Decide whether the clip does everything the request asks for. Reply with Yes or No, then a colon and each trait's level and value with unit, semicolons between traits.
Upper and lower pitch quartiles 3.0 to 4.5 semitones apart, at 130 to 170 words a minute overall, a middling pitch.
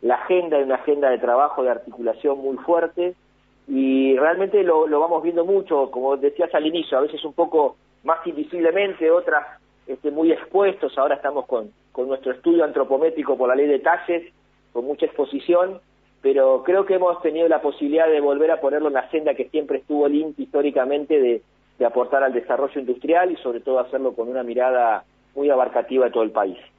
No: average, 4.0 semitones; fast, 190 wpm; medium, 145 Hz